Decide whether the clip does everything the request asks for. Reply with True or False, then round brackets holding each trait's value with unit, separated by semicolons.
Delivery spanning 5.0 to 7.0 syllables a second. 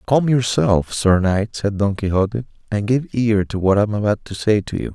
True (5.1 syllables/s)